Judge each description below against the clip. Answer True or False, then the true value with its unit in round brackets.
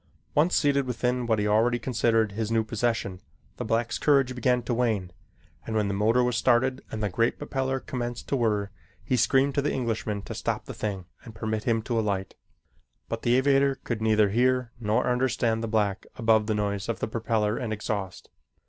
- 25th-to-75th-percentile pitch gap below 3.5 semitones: True (2.6 semitones)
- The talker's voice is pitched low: True (115 Hz)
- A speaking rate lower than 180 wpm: False (195 wpm)